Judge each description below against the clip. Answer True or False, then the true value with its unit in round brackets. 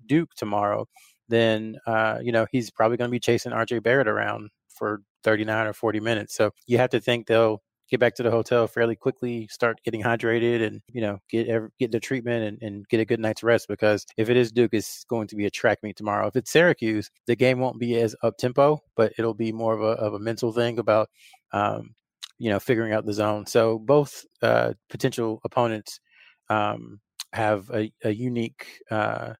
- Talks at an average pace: False (210 wpm)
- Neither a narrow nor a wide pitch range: False (1.8 semitones)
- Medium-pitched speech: False (115 Hz)